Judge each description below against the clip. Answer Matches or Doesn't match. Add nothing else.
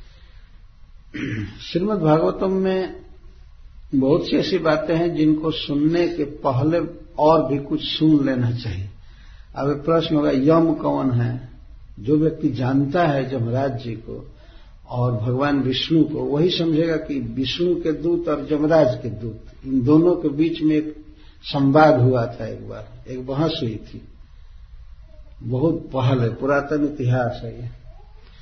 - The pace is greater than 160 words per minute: Doesn't match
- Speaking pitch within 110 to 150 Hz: Matches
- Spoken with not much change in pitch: Doesn't match